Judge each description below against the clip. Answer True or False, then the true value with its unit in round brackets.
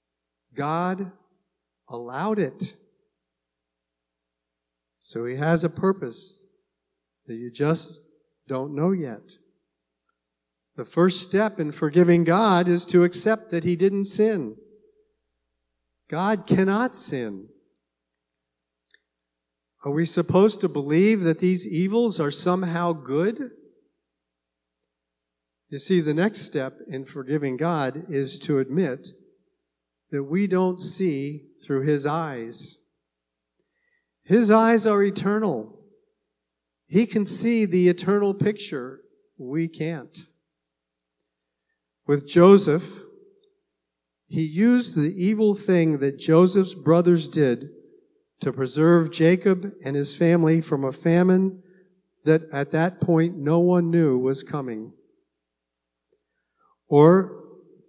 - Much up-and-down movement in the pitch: True (7.5 semitones)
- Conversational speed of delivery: False (105 wpm)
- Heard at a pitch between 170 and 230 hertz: False (160 Hz)